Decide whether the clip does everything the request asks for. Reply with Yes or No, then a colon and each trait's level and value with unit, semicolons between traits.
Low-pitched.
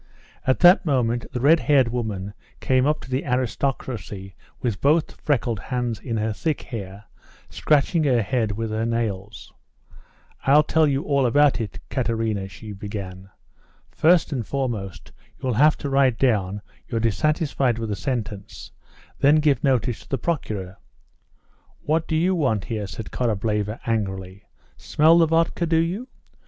Yes: low, 120 Hz